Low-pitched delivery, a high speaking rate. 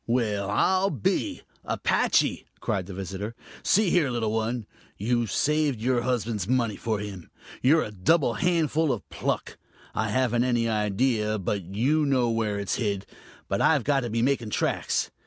No: low, 115 Hz; average, 160 wpm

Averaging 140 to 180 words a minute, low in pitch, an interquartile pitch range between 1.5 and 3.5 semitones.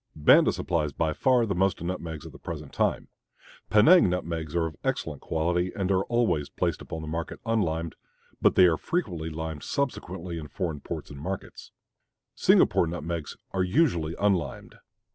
Yes: average, 160 wpm; very low, 85 Hz; average, 3.2 semitones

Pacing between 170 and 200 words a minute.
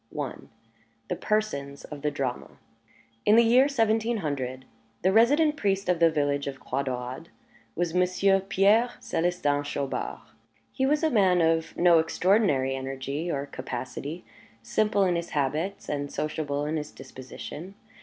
No: average, 145 wpm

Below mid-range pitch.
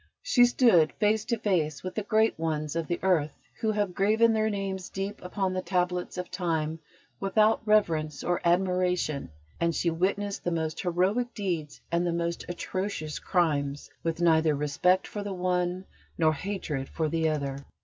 No: medium, 180 Hz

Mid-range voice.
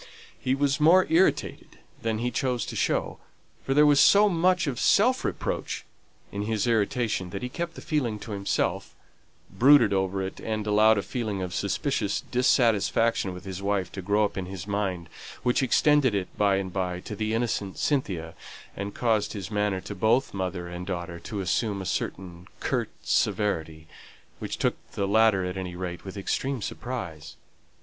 No: low, 105 Hz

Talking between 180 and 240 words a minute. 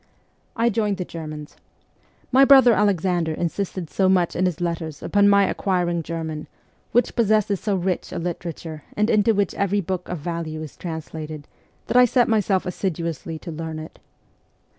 No: average, 160 wpm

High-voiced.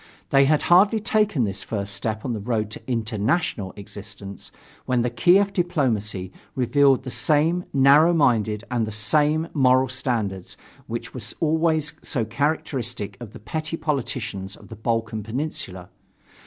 No: low, 125 Hz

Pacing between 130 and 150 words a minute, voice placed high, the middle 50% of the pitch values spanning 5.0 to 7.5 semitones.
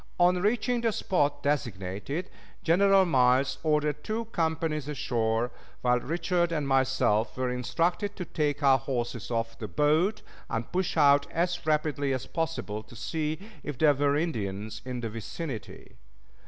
No: average, 145 wpm; medium, 145 Hz; average, 5.3 semitones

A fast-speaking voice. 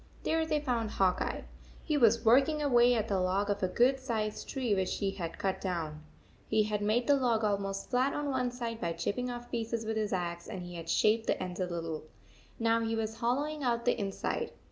Yes: fast, 220 wpm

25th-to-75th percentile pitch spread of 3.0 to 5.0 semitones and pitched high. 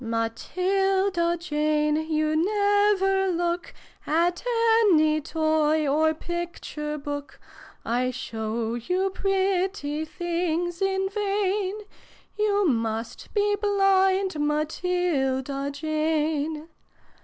Yes: average, 4.3 semitones; very high, 325 Hz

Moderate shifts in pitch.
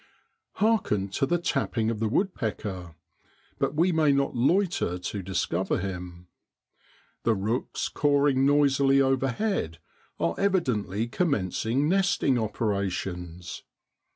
No: wide, 7.2 semitones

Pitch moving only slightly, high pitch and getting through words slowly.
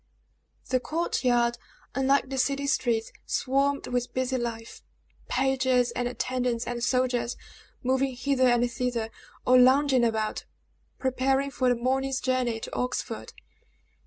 Yes: narrow, 1.6 semitones; very high, 255 Hz; slow, 130 wpm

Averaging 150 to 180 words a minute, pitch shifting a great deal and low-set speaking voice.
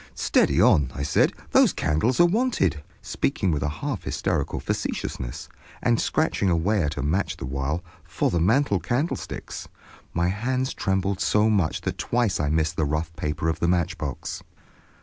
Yes: average, 165 wpm; wide, 6.1 semitones; very low, 85 Hz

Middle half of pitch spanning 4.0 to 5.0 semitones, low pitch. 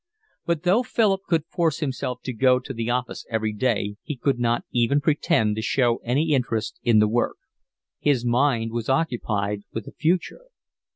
Yes: average, 4.7 semitones; low, 125 Hz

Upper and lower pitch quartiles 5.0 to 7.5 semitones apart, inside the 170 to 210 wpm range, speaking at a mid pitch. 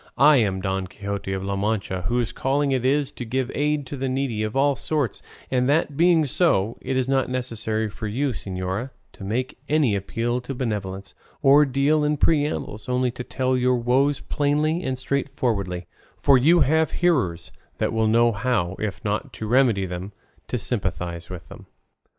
No: average, 5.3 semitones; average, 180 wpm; low, 125 Hz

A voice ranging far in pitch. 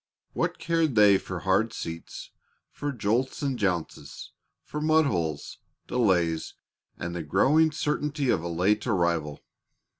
Yes: wide, 8.6 semitones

